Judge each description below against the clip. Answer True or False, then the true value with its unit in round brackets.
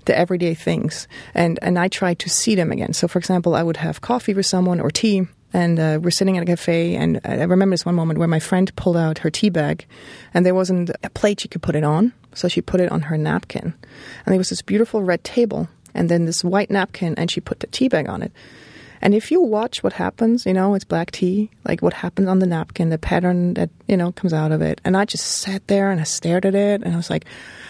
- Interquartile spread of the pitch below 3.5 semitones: True (2.5 semitones)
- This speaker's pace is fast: True (260 wpm)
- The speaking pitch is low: False (180 Hz)